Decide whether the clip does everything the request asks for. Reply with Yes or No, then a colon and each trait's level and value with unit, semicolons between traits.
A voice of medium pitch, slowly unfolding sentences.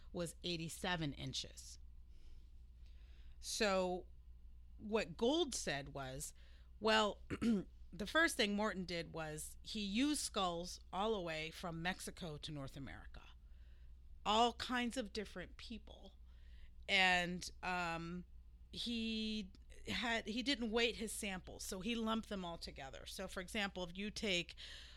Yes: medium, 175 Hz; slow, 125 wpm